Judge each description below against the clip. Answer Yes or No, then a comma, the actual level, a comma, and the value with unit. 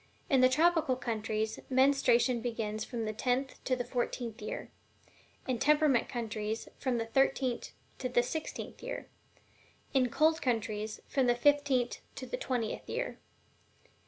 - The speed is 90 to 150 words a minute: Yes, slow, 135 wpm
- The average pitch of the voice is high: Yes, high, 245 Hz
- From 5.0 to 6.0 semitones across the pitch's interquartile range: No, average, 3.0 semitones